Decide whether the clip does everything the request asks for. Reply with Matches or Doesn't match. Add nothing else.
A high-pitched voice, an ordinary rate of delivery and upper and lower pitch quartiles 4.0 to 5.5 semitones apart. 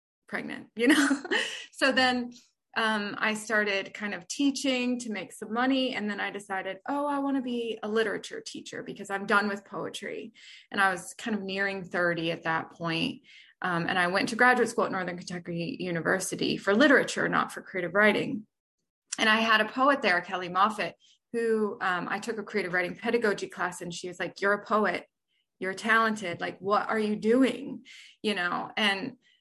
Matches